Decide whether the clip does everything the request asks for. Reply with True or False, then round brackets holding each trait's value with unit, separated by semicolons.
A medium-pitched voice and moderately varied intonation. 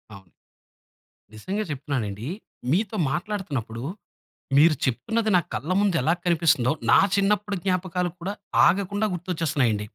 False (170 Hz; 7.2 semitones)